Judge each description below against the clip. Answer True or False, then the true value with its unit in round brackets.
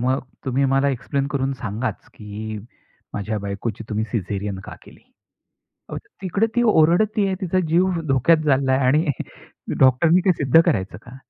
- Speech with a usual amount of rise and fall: False (7.3 semitones)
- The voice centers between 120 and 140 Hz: True (135 Hz)